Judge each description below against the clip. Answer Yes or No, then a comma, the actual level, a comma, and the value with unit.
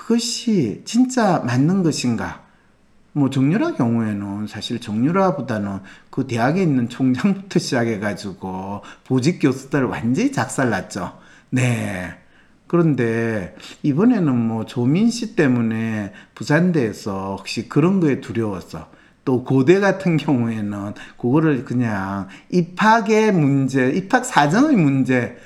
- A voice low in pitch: Yes, low, 130 Hz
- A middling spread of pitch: No, wide, 7.4 semitones